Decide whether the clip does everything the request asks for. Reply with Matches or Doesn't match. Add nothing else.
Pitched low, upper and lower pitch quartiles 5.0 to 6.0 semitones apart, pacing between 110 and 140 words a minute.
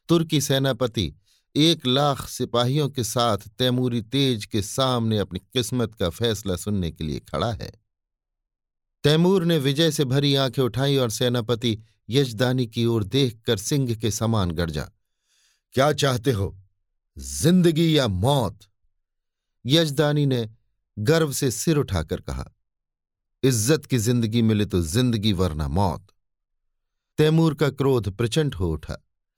Matches